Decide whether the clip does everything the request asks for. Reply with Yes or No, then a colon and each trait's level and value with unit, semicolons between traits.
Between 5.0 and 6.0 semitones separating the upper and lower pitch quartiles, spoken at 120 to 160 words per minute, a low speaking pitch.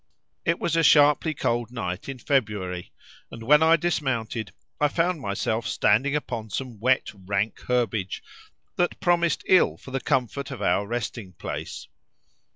Yes: wide, 5.6 semitones; average, 150 wpm; low, 125 Hz